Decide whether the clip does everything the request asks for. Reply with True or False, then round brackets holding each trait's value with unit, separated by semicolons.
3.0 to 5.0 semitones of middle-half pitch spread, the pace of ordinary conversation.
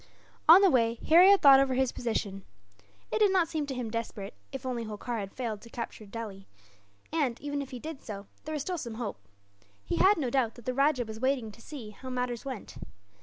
False (4.1 semitones; 220 wpm)